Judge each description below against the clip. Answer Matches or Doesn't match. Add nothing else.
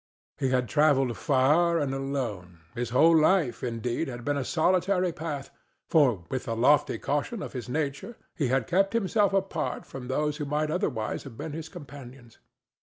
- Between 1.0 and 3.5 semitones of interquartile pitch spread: Doesn't match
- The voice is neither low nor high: Matches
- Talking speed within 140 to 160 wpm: Doesn't match